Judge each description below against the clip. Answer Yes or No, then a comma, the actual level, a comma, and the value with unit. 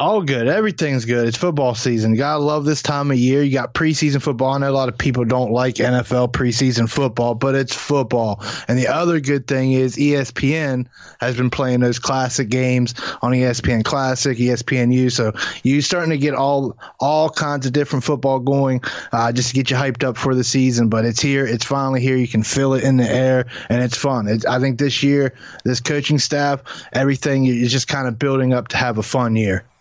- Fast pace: Yes, fast, 215 wpm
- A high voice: No, low, 130 Hz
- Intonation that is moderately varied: No, narrow, 2.1 semitones